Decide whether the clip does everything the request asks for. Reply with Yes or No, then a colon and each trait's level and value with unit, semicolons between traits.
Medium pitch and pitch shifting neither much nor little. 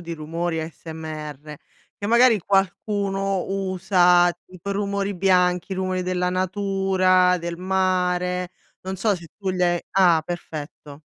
No: medium, 180 Hz; narrow, 1.9 semitones